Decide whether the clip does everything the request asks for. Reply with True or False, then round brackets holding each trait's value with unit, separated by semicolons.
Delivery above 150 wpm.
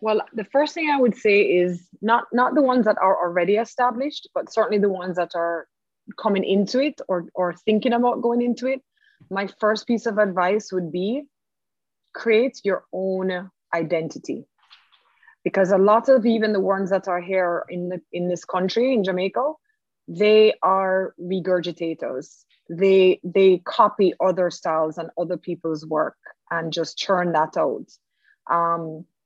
True (160 wpm)